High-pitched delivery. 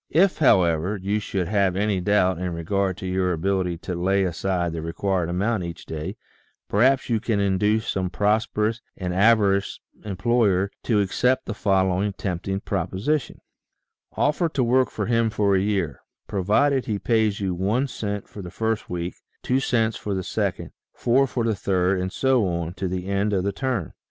No: low, 100 Hz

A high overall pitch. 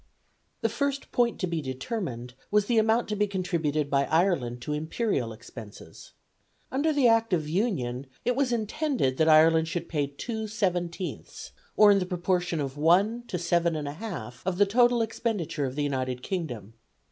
No: medium, 175 Hz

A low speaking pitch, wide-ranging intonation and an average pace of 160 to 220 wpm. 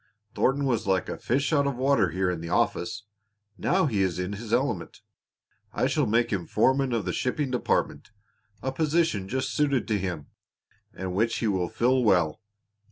Yes: low, 115 Hz; wide, 6.0 semitones; average, 180 wpm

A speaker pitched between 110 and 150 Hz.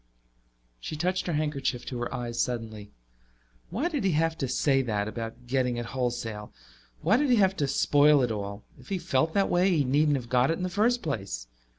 Yes: low, 135 Hz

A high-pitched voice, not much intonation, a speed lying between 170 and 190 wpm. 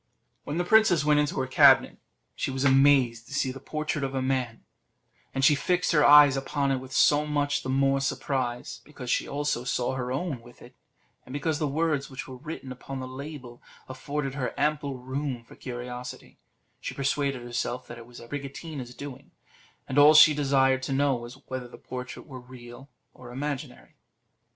No: low, 135 Hz; narrow, 2.3 semitones; average, 185 wpm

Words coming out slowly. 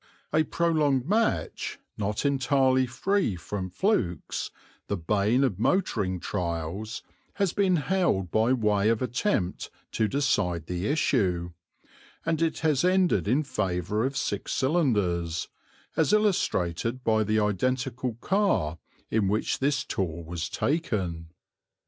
Yes: slow, 125 wpm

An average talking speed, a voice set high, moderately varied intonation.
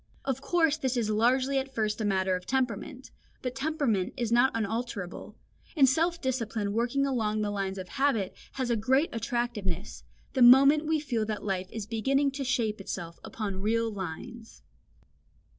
Yes: average, 165 wpm; high, 235 Hz; average, 4.2 semitones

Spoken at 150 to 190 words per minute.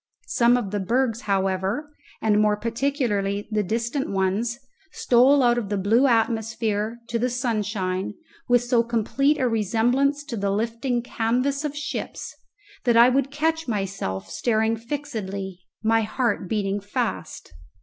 No: average, 140 wpm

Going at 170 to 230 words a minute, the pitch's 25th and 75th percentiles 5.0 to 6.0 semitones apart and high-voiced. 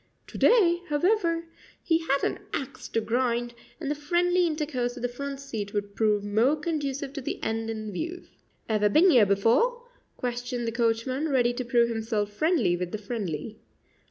Yes: average, 175 wpm; wide, 5.4 semitones; high, 245 Hz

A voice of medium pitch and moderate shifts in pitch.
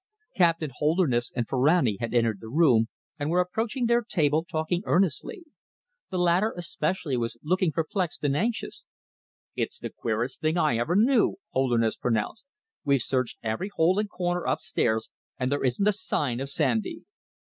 No: medium, 155 Hz; wide, 6.6 semitones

